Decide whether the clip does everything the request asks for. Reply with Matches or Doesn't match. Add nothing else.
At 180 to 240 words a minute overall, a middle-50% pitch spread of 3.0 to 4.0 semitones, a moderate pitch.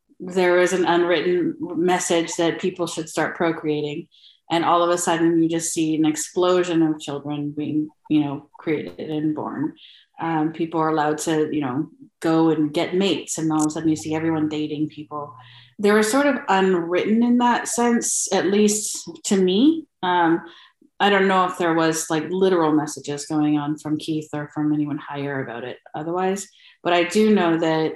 Matches